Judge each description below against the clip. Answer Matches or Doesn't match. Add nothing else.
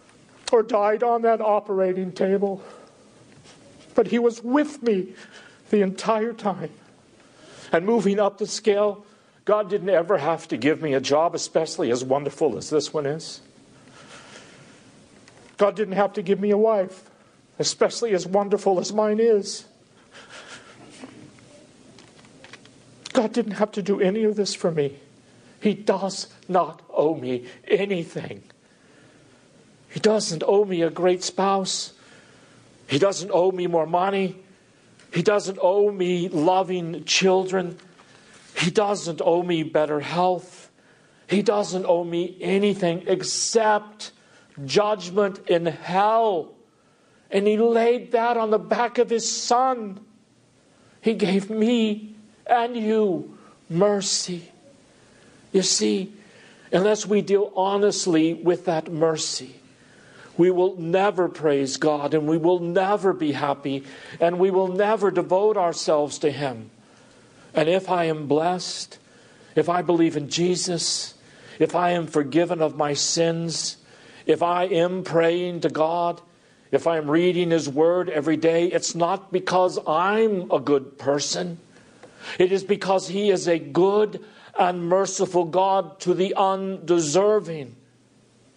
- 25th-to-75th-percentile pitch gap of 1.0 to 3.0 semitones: Doesn't match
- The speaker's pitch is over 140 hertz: Matches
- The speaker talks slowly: Matches